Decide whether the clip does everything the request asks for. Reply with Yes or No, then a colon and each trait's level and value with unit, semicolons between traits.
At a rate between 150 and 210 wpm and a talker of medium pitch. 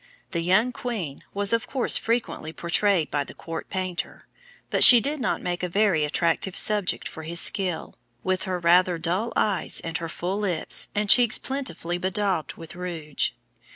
Yes: average, 170 wpm; medium, 180 Hz